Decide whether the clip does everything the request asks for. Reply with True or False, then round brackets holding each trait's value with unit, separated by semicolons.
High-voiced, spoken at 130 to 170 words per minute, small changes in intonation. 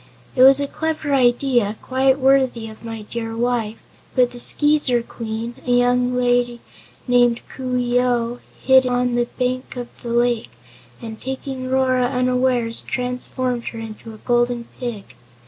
True (245 Hz; 150 wpm; 1.4 semitones)